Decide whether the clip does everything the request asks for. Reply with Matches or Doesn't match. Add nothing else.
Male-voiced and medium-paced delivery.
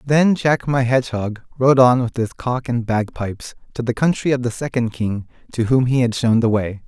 Doesn't match